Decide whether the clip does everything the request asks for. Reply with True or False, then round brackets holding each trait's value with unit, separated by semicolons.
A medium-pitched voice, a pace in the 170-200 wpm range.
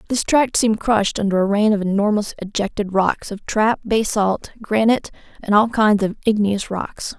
False (210 Hz; 175 wpm)